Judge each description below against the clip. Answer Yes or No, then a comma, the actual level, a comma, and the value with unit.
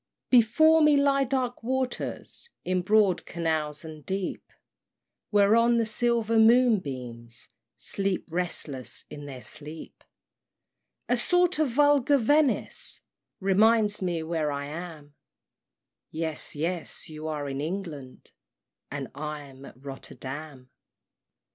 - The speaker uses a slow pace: Yes, slow, 110 wpm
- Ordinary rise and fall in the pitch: No, wide, 8.0 semitones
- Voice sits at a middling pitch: Yes, medium, 180 Hz